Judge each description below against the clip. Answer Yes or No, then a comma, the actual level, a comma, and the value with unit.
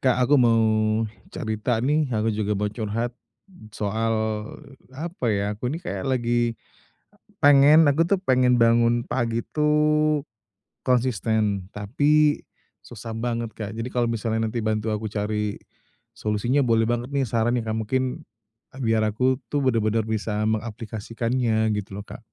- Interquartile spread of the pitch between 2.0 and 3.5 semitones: Yes, average, 2.9 semitones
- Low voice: Yes, low, 115 Hz